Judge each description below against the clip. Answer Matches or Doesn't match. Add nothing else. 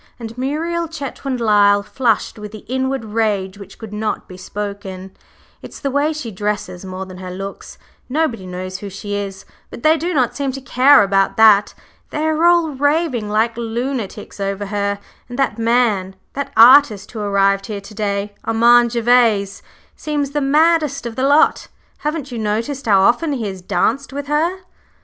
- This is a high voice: Matches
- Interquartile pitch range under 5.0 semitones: Doesn't match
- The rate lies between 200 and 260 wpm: Doesn't match